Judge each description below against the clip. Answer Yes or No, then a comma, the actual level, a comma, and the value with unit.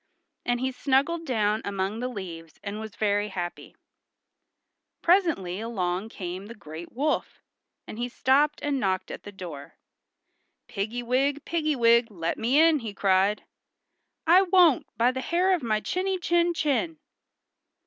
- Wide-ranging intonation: Yes, wide, 7.0 semitones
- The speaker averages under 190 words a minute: Yes, average, 150 wpm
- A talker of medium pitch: No, high, 235 Hz